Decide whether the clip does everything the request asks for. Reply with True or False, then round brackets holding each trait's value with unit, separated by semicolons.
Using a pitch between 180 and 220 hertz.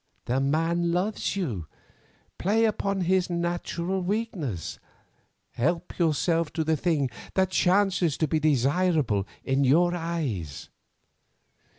False (170 Hz)